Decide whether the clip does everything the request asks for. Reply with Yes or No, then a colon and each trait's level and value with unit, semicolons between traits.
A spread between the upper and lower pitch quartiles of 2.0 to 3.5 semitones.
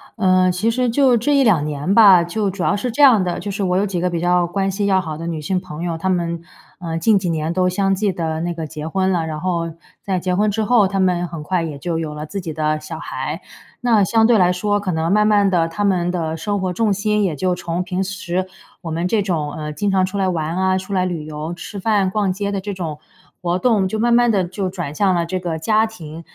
Yes: average, 3.2 semitones